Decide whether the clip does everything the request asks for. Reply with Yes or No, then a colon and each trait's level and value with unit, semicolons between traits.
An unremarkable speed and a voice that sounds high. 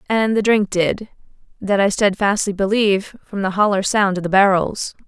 Yes: average, 175 wpm; high, 200 Hz